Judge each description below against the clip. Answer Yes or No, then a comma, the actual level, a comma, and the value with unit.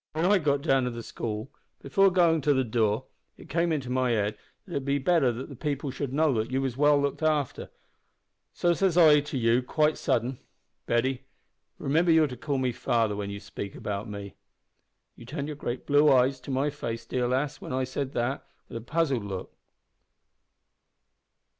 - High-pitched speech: No, low, 135 Hz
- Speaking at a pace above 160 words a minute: Yes, average, 195 wpm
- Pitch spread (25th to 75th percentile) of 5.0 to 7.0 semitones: No, average, 3.9 semitones